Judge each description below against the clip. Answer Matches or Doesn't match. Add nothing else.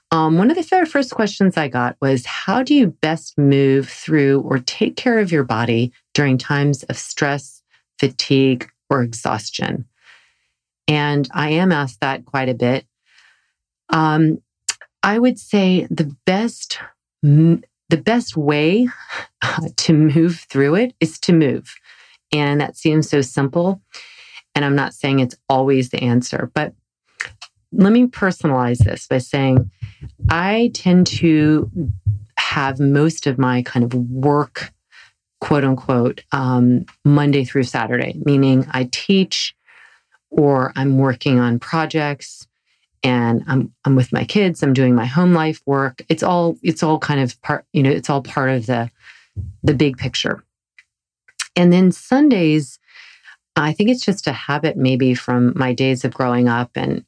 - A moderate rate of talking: Matches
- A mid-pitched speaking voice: Matches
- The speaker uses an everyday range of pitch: Matches